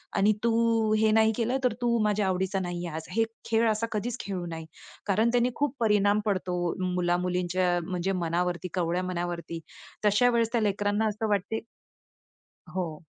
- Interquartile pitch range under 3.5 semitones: No, average, 3.8 semitones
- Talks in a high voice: Yes, high, 205 Hz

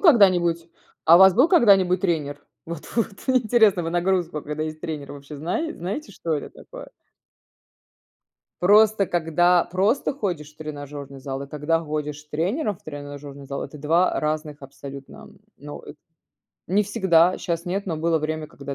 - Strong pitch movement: No, average, 4.2 semitones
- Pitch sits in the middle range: Yes, medium, 165 Hz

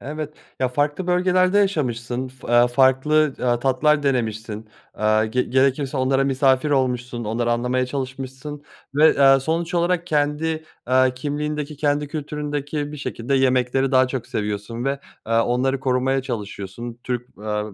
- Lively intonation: No, average, 3.2 semitones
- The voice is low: Yes, low, 130 Hz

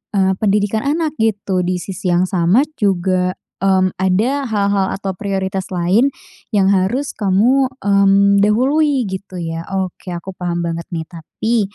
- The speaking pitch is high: Yes, high, 195 Hz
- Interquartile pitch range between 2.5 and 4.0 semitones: Yes, average, 2.8 semitones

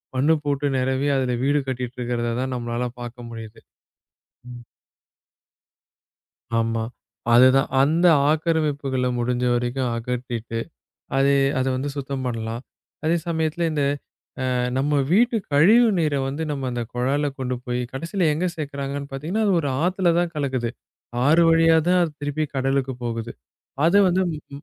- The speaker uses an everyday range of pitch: Yes, average, 4.1 semitones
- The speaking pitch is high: No, low, 135 Hz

